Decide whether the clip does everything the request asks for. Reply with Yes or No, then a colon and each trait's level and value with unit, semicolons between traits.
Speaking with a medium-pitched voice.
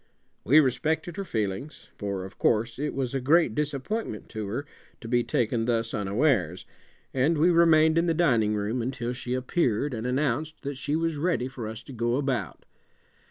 No: low, 130 Hz